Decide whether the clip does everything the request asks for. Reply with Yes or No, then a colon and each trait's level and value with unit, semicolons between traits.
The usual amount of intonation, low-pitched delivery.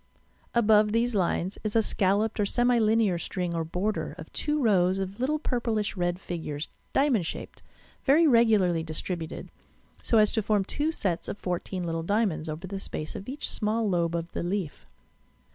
No: average, 4.4 semitones; high, 200 Hz